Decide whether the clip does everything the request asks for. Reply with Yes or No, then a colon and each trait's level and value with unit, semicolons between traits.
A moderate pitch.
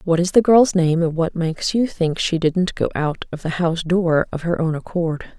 Yes: medium, 170 Hz